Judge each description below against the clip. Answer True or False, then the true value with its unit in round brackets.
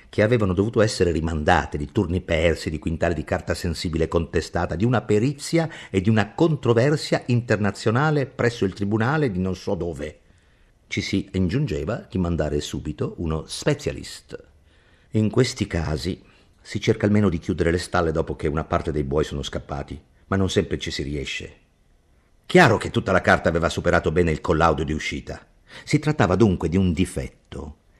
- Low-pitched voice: True (90 Hz)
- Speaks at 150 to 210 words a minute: True (170 wpm)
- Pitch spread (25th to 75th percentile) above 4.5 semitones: True (4.9 semitones)